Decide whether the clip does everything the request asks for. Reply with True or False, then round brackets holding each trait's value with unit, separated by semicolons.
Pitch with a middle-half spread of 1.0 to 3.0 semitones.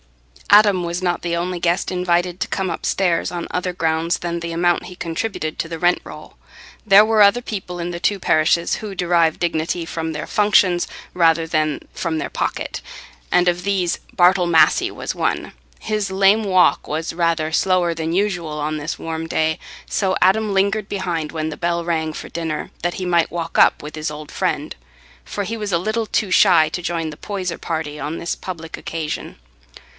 True (2.4 semitones)